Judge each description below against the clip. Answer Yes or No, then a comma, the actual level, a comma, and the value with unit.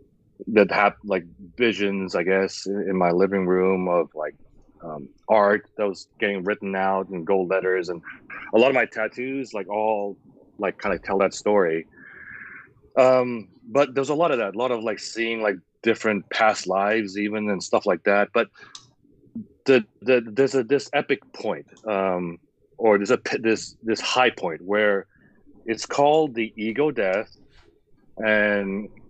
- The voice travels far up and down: No, average, 3.6 semitones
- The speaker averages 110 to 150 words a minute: No, average, 165 wpm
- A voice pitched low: Yes, low, 105 Hz